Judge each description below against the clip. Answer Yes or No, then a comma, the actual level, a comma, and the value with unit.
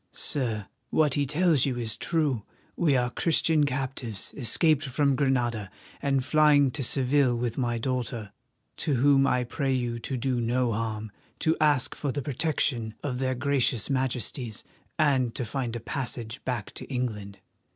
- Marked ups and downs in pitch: No, average, 3.2 semitones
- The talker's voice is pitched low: Yes, low, 130 Hz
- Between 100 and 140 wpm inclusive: No, average, 160 wpm